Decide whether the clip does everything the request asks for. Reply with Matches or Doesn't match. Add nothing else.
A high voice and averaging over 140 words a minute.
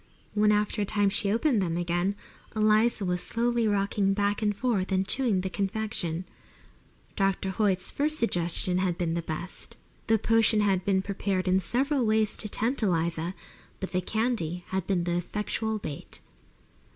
Matches